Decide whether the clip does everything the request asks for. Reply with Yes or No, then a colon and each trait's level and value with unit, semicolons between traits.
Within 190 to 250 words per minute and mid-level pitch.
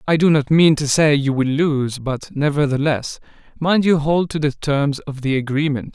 Yes: average, 200 wpm; medium, 145 Hz